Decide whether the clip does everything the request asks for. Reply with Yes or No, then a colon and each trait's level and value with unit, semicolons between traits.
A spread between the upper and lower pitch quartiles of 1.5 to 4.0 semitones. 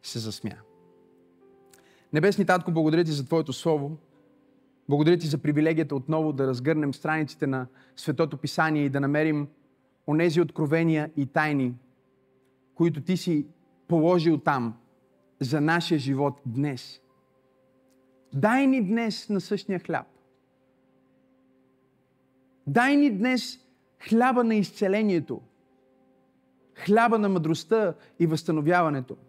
No: average, 4.5 semitones